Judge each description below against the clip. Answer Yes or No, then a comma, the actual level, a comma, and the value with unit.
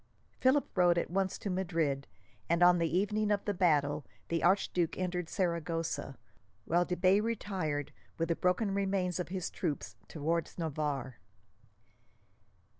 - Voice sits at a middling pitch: Yes, medium, 175 Hz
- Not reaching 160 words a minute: Yes, average, 140 wpm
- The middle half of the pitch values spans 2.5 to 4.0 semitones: Yes, average, 3.0 semitones